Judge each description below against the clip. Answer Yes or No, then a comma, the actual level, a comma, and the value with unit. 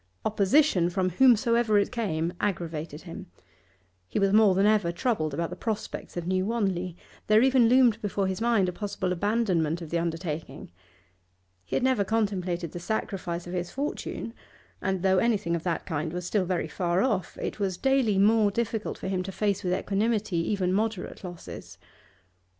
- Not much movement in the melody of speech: No, average, 3.8 semitones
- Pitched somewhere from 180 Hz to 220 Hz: Yes, high, 190 Hz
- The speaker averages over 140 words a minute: Yes, average, 175 wpm